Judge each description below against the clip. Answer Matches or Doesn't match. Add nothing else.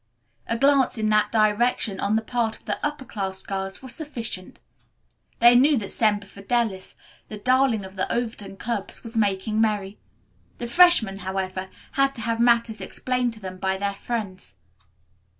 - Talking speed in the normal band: Matches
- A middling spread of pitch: Matches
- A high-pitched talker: Matches